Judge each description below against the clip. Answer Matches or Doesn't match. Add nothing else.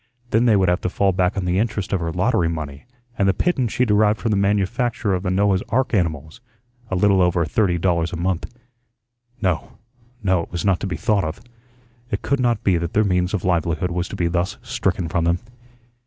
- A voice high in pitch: Doesn't match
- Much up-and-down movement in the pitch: Doesn't match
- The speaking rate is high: Matches